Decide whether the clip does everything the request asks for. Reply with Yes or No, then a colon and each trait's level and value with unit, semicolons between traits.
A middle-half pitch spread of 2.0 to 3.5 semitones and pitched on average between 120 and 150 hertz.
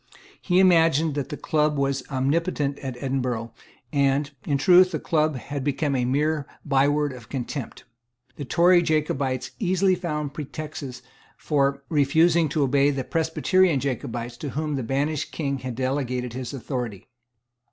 Yes: average, 2.9 semitones; medium, 140 Hz